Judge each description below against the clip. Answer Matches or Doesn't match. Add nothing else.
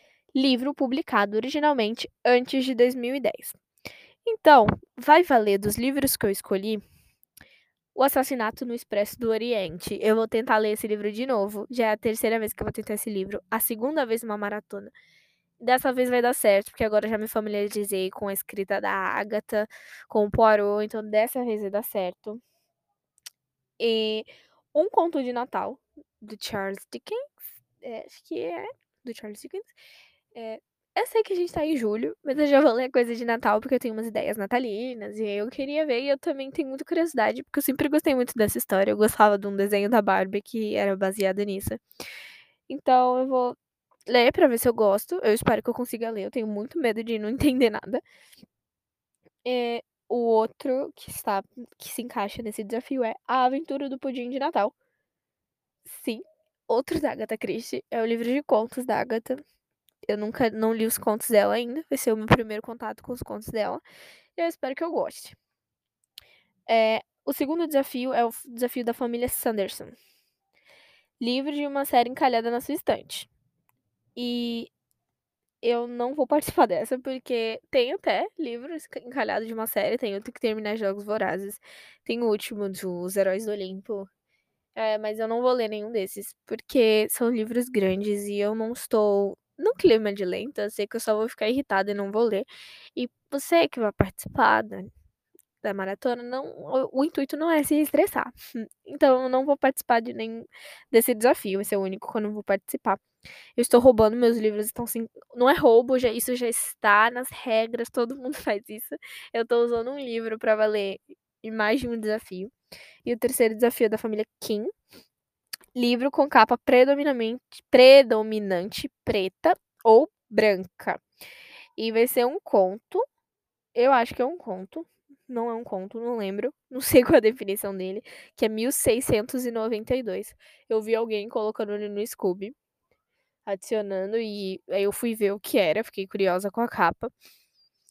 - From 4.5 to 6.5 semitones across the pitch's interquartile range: Doesn't match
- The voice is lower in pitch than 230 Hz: Doesn't match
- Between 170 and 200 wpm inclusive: Matches